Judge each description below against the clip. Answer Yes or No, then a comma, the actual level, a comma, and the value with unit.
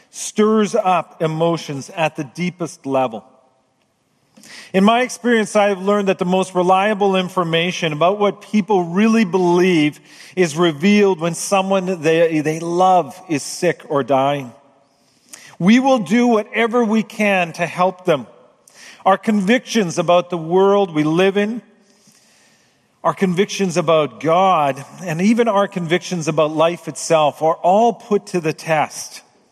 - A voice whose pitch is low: No, medium, 180 Hz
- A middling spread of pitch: Yes, average, 4.0 semitones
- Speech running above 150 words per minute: No, average, 140 wpm